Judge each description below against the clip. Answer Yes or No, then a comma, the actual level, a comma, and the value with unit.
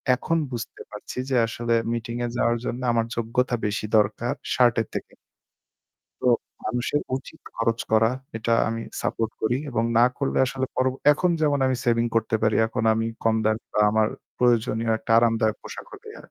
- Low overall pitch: Yes, low, 115 Hz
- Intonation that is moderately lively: No, narrow, 1.7 semitones